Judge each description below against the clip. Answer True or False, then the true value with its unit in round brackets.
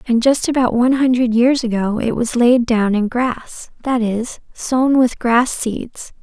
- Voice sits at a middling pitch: False (240 Hz)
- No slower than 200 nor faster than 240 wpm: False (185 wpm)